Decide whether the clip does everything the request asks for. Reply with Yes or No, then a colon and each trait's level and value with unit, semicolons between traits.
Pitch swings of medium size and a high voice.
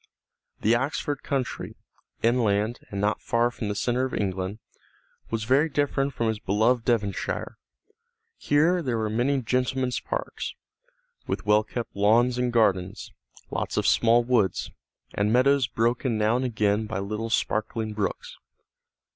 No: average, 3.0 semitones; low, 115 Hz